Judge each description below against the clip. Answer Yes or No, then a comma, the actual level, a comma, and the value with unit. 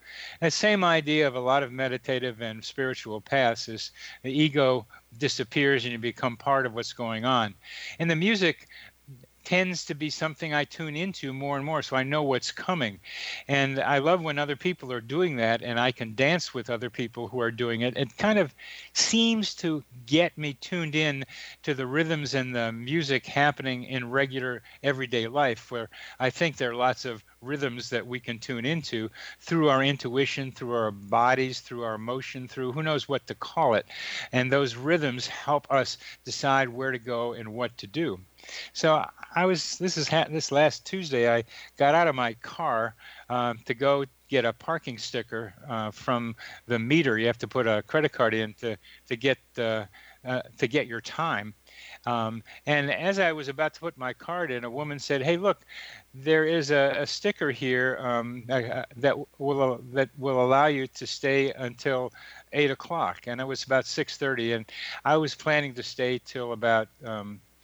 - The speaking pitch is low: Yes, low, 130 Hz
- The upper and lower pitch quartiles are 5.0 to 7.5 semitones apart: No, average, 3.7 semitones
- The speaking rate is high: No, average, 190 wpm